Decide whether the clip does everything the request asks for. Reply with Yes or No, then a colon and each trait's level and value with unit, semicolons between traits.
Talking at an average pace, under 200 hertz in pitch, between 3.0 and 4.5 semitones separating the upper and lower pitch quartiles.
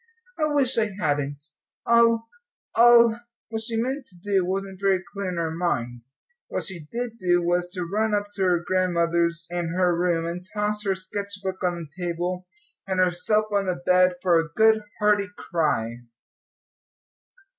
Yes: average, 170 wpm; medium, 185 Hz; average, 3.5 semitones